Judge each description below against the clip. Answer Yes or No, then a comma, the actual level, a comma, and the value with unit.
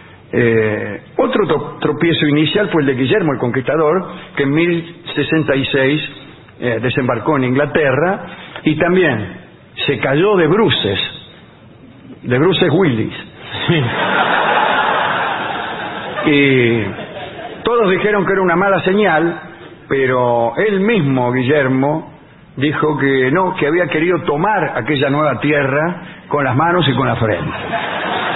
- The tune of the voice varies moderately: Yes, average, 4.2 semitones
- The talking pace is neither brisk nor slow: No, slow, 120 wpm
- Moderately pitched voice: Yes, medium, 150 Hz